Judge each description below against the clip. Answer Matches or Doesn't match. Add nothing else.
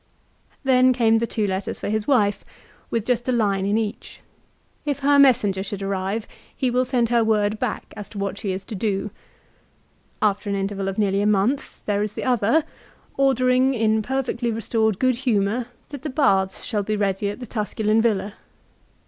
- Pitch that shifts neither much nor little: Matches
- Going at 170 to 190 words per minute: Matches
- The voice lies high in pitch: Matches